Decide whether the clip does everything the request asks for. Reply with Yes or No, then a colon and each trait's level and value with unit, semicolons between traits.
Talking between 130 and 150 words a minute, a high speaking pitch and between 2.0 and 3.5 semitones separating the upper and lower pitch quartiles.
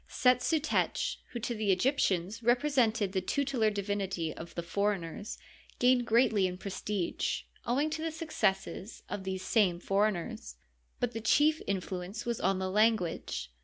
No: average, 145 wpm; high, 210 Hz; average, 4.5 semitones